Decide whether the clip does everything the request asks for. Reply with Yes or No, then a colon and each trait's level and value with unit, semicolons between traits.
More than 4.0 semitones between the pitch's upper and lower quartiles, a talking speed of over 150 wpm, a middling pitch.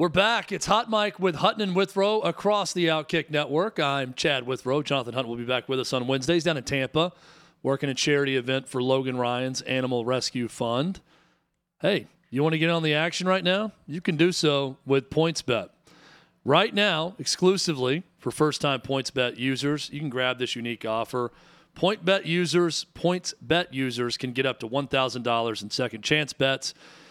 Yes: average, 5.0 semitones; average, 185 wpm; medium, 145 Hz